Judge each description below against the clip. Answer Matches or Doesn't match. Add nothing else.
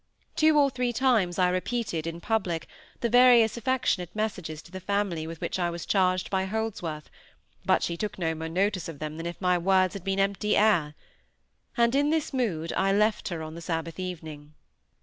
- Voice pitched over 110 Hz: Matches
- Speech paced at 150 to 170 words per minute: Doesn't match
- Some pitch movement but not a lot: Matches